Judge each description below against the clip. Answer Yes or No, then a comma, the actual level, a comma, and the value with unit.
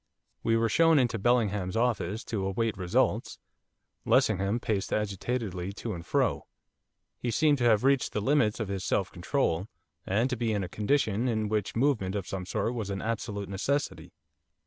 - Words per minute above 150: Yes, average, 170 wpm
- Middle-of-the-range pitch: No, low, 110 Hz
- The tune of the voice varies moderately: Yes, average, 3.7 semitones